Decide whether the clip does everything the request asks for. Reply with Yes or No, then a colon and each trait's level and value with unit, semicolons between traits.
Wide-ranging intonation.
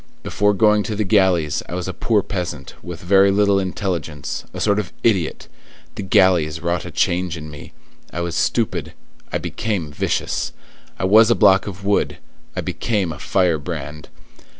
No: average, 3.3 semitones